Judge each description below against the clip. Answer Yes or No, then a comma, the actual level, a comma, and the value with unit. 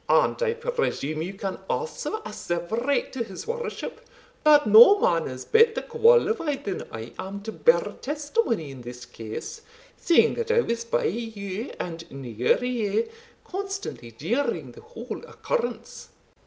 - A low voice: No, high, 235 Hz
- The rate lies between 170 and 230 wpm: No, average, 140 wpm